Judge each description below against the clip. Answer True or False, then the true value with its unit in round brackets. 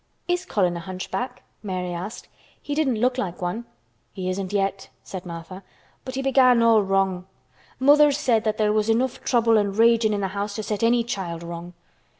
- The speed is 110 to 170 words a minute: False (185 wpm)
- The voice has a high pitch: True (210 Hz)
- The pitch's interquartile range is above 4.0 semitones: True (4.4 semitones)